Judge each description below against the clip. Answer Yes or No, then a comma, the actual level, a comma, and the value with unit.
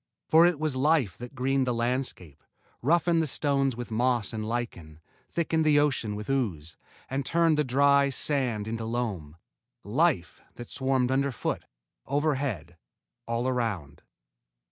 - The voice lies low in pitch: Yes, low, 130 Hz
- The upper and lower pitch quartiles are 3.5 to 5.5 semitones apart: Yes, average, 4.2 semitones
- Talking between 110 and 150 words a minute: Yes, average, 140 wpm